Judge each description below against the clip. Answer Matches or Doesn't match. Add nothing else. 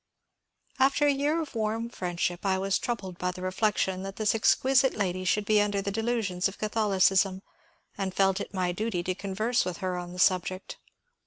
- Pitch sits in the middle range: Doesn't match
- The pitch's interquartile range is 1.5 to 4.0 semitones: Matches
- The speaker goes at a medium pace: Matches